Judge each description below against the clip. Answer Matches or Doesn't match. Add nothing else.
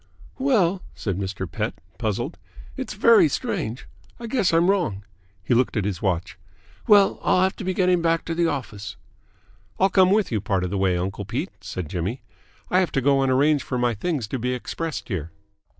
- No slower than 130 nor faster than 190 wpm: Doesn't match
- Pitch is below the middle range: Matches